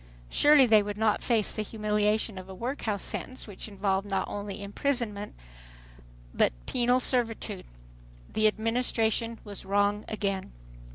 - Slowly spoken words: Yes, slow, 130 wpm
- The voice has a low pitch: No, high, 210 Hz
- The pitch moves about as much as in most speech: No, narrow, 2.3 semitones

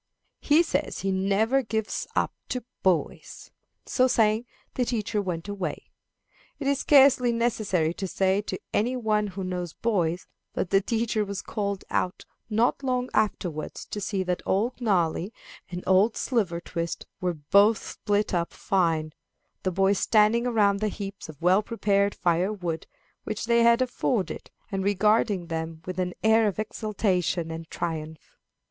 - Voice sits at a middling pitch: No, high, 200 Hz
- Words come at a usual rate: Yes, average, 155 wpm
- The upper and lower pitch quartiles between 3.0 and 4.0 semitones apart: Yes, average, 3.7 semitones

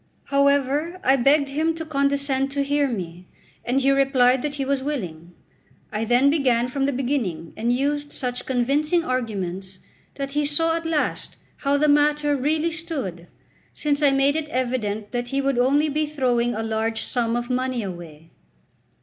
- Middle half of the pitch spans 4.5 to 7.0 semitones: No, average, 3.3 semitones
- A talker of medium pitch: No, very high, 270 Hz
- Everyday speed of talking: Yes, average, 170 wpm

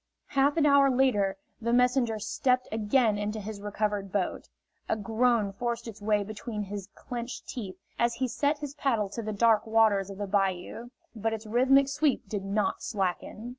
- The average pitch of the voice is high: Yes, high, 220 Hz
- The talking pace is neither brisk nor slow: Yes, average, 175 wpm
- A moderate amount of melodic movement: Yes, average, 3.3 semitones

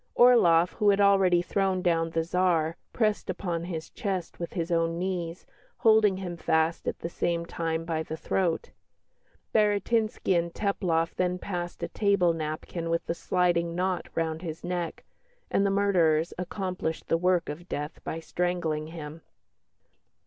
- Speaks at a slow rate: No, average, 155 wpm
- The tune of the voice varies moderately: No, narrow, 2.3 semitones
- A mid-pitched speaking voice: Yes, medium, 175 Hz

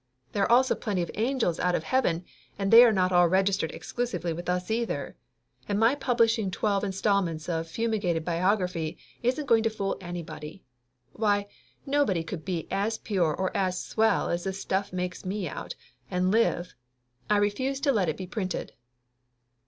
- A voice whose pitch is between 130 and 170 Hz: No, high, 195 Hz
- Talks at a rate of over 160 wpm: Yes, average, 170 wpm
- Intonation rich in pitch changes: No, average, 4.0 semitones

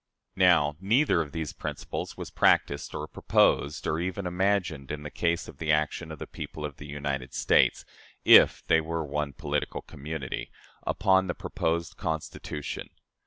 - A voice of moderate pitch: No, very low, 80 Hz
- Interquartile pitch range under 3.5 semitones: Yes, average, 2.9 semitones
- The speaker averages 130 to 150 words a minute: No, average, 160 wpm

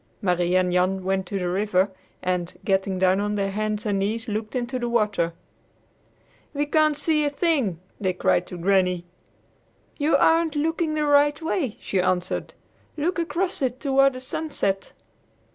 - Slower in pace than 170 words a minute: Yes, average, 160 wpm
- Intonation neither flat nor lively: No, wide, 7.6 semitones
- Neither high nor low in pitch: No, high, 215 Hz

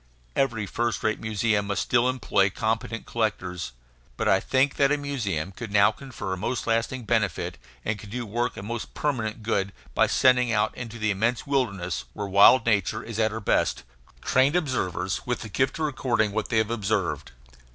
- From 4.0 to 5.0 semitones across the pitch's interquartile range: No, average, 3.5 semitones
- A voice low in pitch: Yes, low, 110 Hz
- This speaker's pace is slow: No, average, 185 wpm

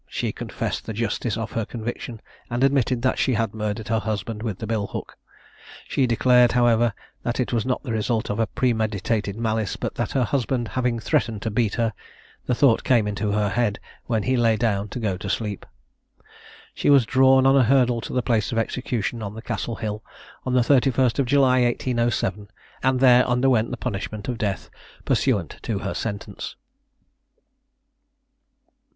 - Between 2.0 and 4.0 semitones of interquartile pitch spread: Yes, narrow, 2.6 semitones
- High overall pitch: No, low, 115 Hz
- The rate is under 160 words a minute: No, average, 180 wpm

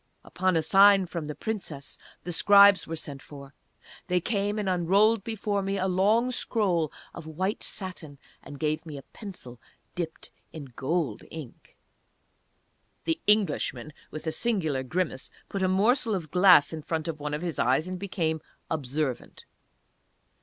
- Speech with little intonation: No, average, 4.5 semitones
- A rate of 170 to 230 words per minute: No, average, 155 wpm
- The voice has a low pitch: No, medium, 175 Hz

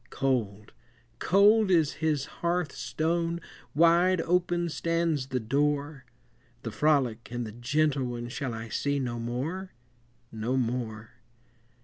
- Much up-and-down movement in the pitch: Yes, wide, 5.7 semitones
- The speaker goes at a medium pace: No, slow, 120 wpm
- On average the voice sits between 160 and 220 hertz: No, medium, 140 Hz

